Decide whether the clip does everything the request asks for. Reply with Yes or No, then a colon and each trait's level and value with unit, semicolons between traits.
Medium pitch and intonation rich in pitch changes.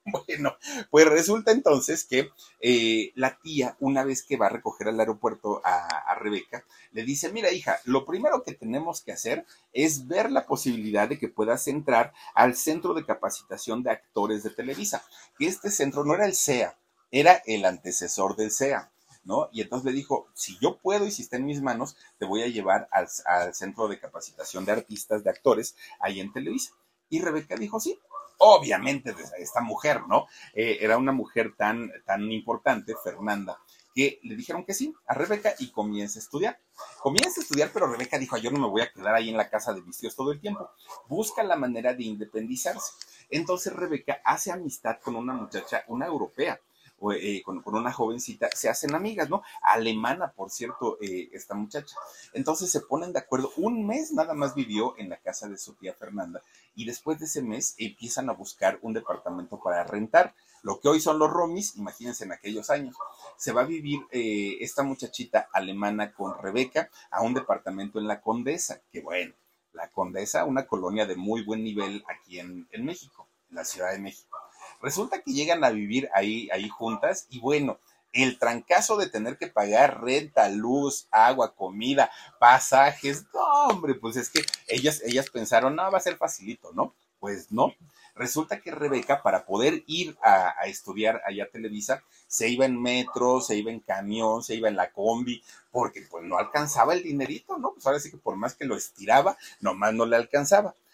No: low, 130 Hz; wide, 6.4 semitones